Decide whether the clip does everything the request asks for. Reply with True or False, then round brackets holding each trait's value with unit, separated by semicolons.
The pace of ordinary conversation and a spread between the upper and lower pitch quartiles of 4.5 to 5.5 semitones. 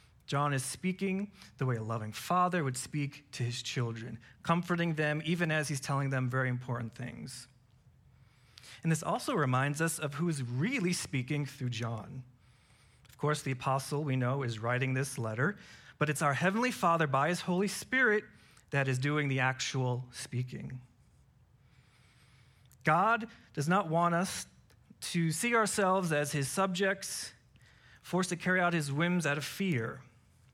True (155 wpm; 5.1 semitones)